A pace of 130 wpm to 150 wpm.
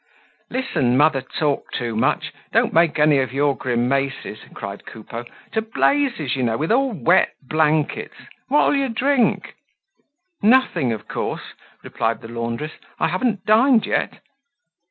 Yes: slow, 135 wpm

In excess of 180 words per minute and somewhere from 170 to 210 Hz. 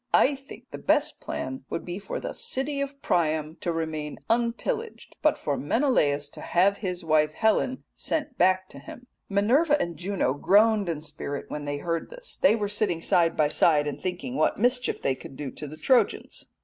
Yes: average, 190 wpm; medium, 185 Hz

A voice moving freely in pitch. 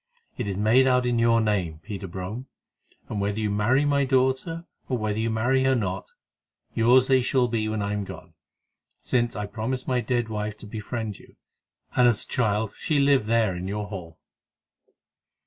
No: average, 3.6 semitones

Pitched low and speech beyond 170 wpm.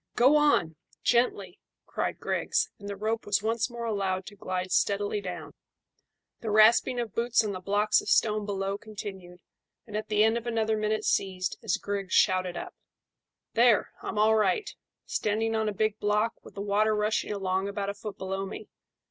No: high, 210 Hz; average, 180 wpm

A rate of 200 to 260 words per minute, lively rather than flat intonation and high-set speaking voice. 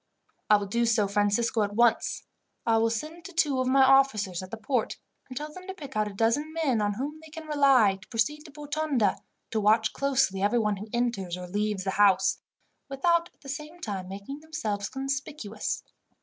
Yes: fast, 205 wpm; wide, 5.9 semitones; high, 235 Hz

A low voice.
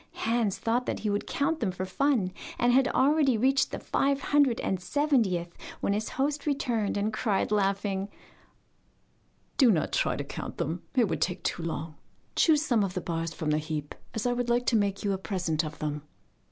No: high, 210 Hz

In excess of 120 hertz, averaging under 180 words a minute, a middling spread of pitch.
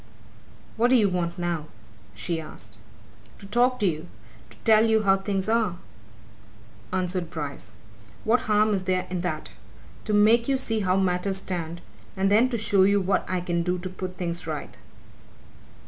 Yes: high, 190 Hz; average, 170 wpm; average, 3.5 semitones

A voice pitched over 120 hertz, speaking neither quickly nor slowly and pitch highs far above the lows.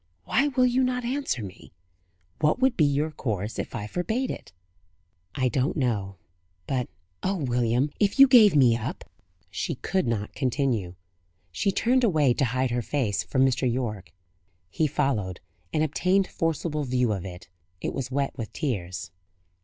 Yes: low, 135 Hz; average, 170 wpm; wide, 7.2 semitones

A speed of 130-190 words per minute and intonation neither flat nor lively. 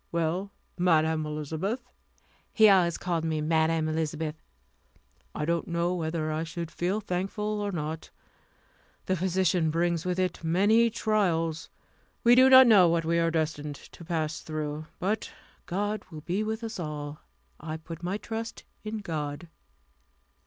Yes: average, 145 wpm; average, 3.7 semitones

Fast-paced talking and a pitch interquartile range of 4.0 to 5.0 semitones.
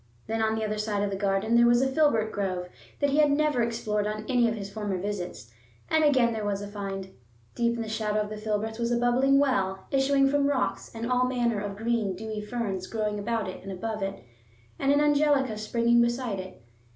No: fast, 225 wpm; average, 3.3 semitones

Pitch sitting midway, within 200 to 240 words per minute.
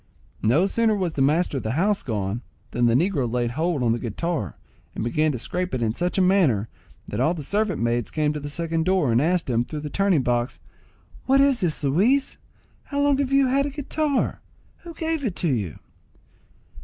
Yes: medium, 160 Hz; fast, 205 wpm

